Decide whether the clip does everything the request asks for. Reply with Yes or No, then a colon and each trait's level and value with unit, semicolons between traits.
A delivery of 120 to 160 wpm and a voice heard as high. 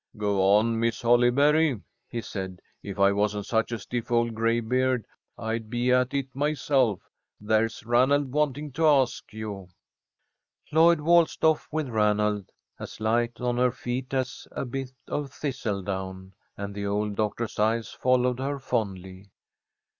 No: average, 150 wpm; low, 120 Hz